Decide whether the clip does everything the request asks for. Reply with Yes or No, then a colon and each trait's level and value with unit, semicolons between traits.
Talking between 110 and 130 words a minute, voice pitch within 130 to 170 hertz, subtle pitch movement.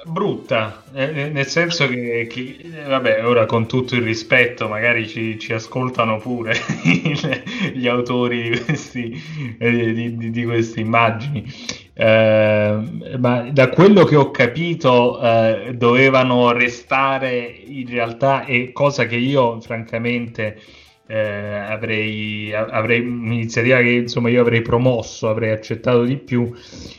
No: average, 120 wpm; low, 120 Hz; narrow, 2.3 semitones